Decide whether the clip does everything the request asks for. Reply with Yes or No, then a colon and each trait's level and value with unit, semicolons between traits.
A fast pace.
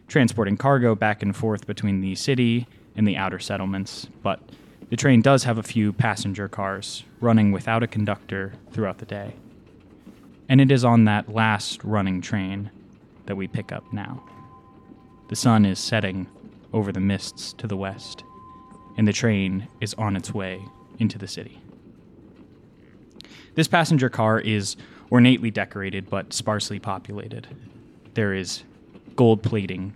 No: average, 150 wpm